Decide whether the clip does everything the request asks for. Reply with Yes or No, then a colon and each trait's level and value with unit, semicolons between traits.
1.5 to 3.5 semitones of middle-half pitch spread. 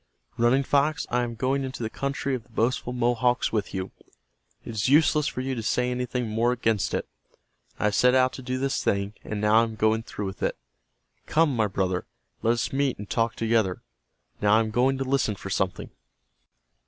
Yes: average, 3.1 semitones